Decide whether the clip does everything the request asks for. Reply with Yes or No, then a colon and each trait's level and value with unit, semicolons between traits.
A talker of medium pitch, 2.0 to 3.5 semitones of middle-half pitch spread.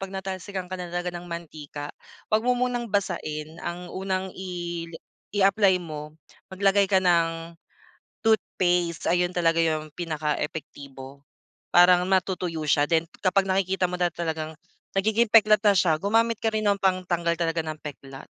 Yes: medium, 180 Hz; average, 2.9 semitones